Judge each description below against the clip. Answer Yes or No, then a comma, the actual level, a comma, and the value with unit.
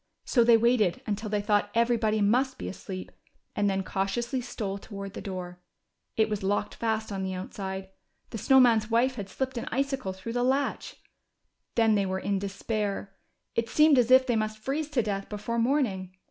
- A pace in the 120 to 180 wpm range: No, average, 190 wpm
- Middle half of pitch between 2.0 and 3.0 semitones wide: No, average, 3.6 semitones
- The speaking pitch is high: Yes, high, 215 Hz